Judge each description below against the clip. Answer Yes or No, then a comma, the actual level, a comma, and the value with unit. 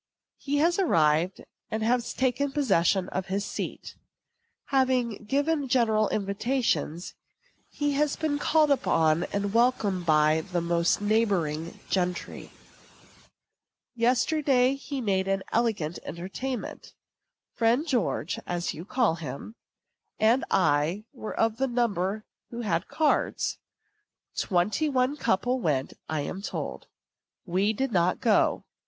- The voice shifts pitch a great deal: Yes, wide, 6.5 semitones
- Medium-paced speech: No, slow, 120 wpm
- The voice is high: Yes, high, 215 Hz